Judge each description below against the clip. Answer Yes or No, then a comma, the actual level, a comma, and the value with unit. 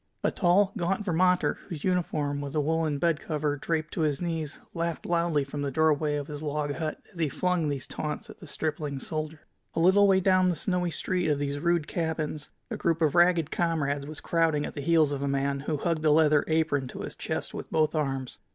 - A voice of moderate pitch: Yes, medium, 155 Hz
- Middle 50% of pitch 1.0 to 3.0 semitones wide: Yes, average, 2.7 semitones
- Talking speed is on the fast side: Yes, fast, 215 wpm